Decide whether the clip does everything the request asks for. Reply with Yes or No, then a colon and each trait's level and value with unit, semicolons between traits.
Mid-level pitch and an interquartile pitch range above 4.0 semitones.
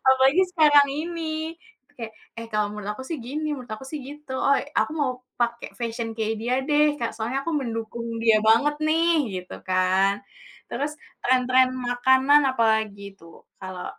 No: very high, 250 Hz; average, 4.8 semitones